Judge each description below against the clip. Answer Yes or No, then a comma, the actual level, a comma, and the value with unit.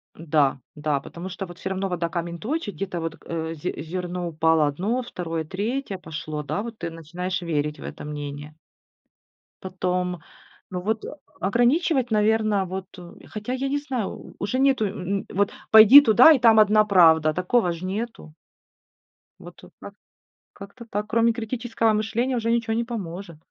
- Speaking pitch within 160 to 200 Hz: Yes, high, 190 Hz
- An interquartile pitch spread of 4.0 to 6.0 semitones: Yes, average, 5.3 semitones